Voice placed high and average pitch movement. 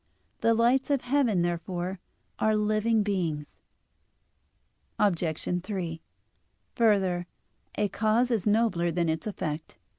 Yes: high, 200 Hz; average, 4.3 semitones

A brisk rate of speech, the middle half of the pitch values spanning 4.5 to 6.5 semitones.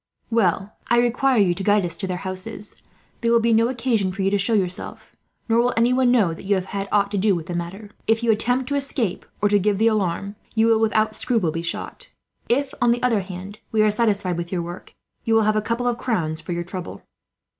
No: fast, 240 wpm; average, 3.7 semitones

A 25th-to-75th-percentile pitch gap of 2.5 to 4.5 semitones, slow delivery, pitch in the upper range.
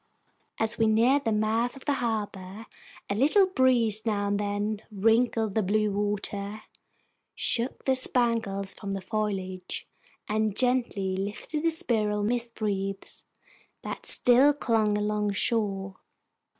Yes: average, 2.8 semitones; slow, 130 wpm; high, 215 Hz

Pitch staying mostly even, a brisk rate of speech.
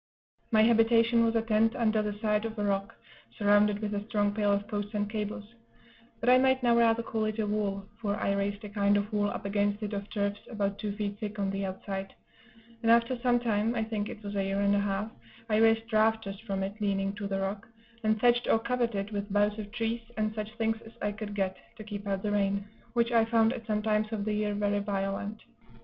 Yes: narrow, 1.8 semitones; fast, 235 wpm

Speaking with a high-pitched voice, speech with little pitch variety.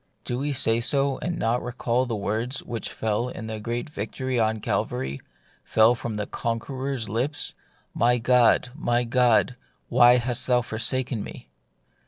No: low, 120 Hz; narrow, 2.3 semitones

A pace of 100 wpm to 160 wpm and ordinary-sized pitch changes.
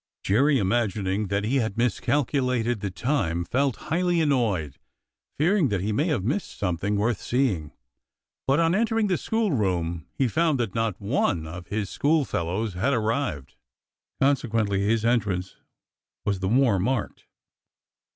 No: average, 145 wpm; wide, 6.1 semitones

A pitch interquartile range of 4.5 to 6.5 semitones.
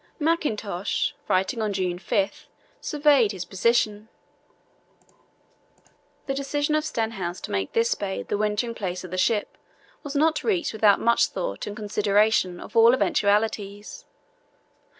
No: average, 3.7 semitones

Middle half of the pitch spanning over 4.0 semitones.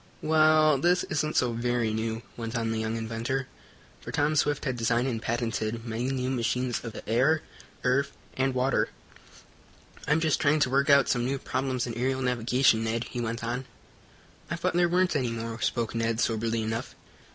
No: average, 3.2 semitones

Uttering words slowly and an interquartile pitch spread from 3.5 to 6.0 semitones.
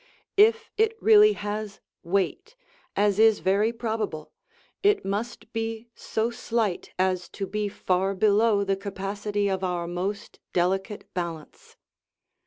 No: slow, 125 wpm; average, 2.9 semitones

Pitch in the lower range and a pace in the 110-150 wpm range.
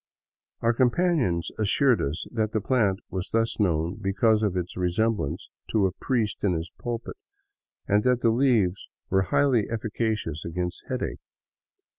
Yes: low, 105 Hz; average, 145 wpm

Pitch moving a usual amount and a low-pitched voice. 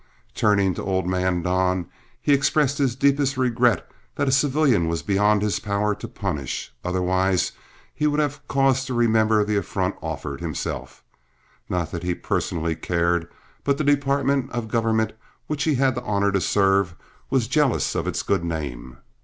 No: wide, 6.7 semitones; low, 105 Hz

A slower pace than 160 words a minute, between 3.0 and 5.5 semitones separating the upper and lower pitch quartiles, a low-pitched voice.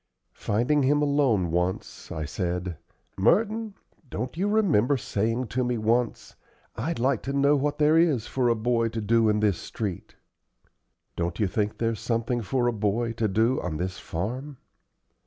No: average, 165 wpm; average, 4.9 semitones; low, 115 Hz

